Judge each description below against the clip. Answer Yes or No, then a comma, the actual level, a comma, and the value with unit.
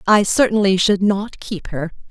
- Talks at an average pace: Yes, average, 170 wpm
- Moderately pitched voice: No, high, 200 Hz